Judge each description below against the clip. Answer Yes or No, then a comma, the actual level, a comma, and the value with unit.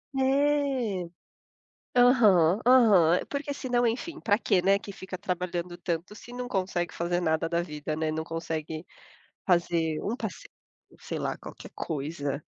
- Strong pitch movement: Yes, wide, 6.7 semitones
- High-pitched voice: No, medium, 180 Hz